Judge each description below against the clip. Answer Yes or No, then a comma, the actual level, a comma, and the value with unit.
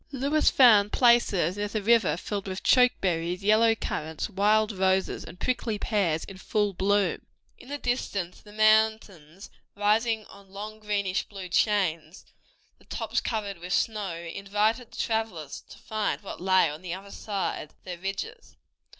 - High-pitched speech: Yes, high, 205 Hz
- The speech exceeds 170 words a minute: No, average, 160 wpm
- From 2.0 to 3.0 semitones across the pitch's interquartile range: Yes, average, 2.7 semitones